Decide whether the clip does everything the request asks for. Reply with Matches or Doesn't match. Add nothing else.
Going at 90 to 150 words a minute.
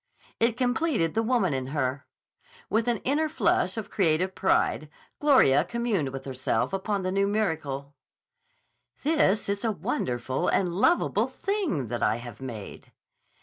Matches